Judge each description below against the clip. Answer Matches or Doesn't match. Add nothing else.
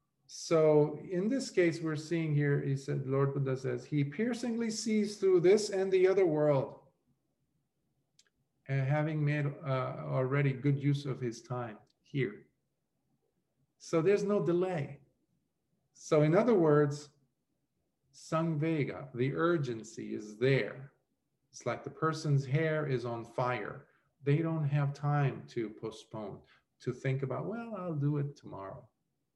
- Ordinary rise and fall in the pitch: Matches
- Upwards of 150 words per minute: Doesn't match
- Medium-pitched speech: Matches